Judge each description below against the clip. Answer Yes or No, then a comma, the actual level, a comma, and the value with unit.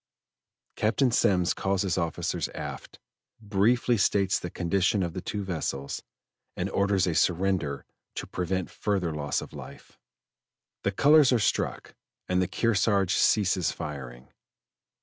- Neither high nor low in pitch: No, very low, 95 Hz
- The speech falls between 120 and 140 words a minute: Yes, slow, 135 wpm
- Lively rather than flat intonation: No, average, 2.9 semitones